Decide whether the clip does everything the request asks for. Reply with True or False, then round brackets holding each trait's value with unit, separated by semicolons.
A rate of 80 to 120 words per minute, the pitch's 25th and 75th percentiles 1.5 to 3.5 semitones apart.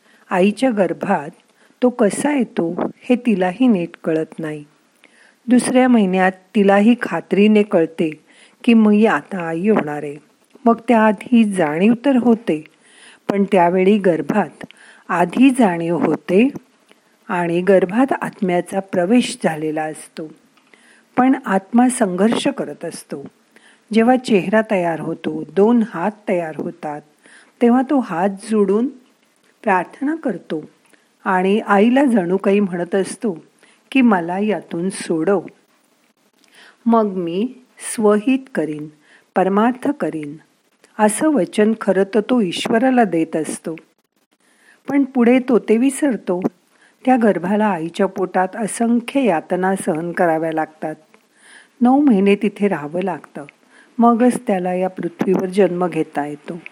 False (115 wpm; 5.1 semitones)